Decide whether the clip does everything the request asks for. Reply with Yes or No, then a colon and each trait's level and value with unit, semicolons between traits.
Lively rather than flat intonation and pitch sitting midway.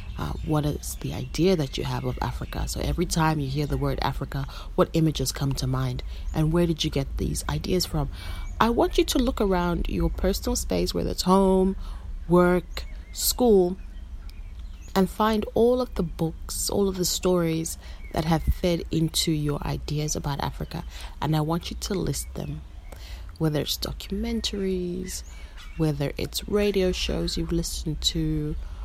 Yes: wide, 5.9 semitones; medium, 160 Hz